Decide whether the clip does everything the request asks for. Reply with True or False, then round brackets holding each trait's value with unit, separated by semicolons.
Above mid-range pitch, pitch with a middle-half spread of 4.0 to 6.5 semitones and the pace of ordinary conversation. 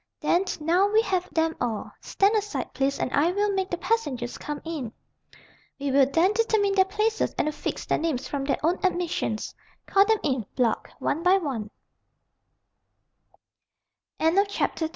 True (335 Hz; 6.2 semitones; 150 wpm)